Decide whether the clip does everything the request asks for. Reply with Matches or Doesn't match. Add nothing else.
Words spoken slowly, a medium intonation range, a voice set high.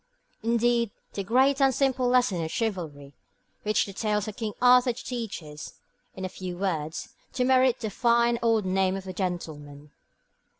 Doesn't match